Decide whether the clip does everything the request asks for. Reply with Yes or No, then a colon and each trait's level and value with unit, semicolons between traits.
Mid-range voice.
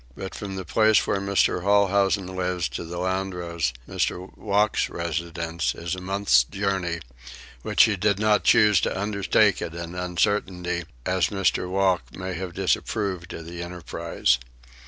No: very low, 95 Hz